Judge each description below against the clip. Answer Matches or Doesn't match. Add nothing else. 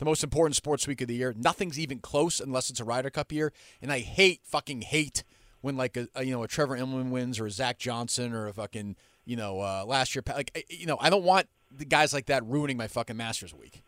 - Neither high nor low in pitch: Doesn't match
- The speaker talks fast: Matches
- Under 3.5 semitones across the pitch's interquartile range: Doesn't match